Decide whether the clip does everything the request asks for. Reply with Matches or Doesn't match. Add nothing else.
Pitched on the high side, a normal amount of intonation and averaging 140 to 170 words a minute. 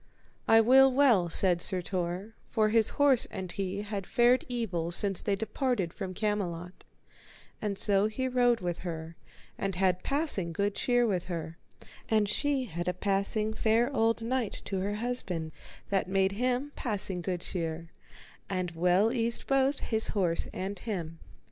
Matches